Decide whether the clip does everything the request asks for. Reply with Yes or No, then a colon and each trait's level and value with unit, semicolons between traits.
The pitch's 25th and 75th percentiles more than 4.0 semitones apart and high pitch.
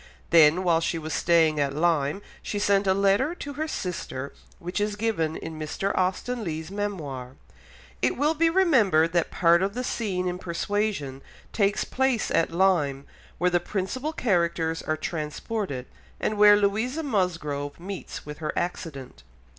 No: average, 4.7 semitones; medium, 180 Hz